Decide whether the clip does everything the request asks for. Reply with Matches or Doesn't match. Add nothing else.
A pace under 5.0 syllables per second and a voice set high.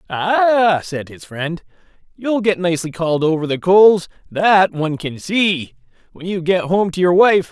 Doesn't match